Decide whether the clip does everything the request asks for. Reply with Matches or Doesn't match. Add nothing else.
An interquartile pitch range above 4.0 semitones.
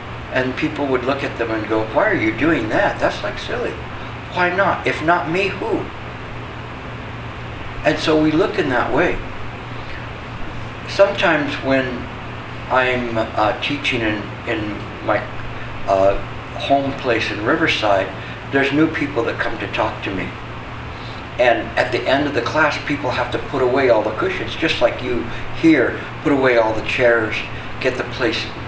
Doesn't match